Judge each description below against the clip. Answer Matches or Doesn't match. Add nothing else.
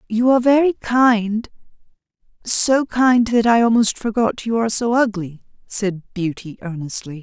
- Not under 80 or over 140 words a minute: Matches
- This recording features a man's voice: Doesn't match